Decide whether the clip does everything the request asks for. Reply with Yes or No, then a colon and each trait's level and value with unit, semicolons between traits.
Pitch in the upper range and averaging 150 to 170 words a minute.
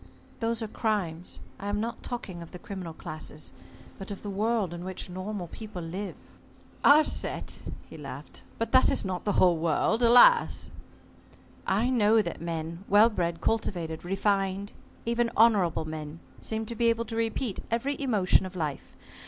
Yes: high, 200 Hz; average, 165 wpm